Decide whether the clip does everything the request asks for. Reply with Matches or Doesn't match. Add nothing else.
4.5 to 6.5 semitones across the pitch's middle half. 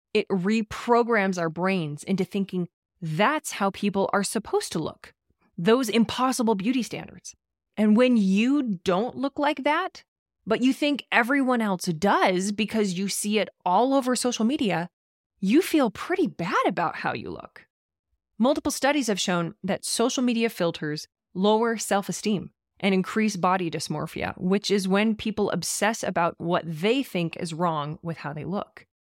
Matches